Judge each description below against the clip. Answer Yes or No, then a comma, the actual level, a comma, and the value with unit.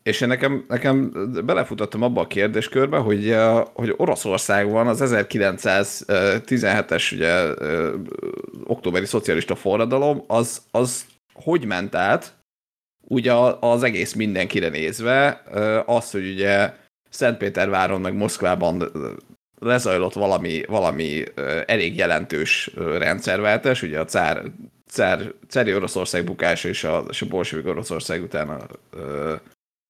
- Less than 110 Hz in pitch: No, low, 115 Hz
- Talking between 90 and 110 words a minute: Yes, slow, 105 wpm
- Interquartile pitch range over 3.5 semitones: Yes, average, 3.9 semitones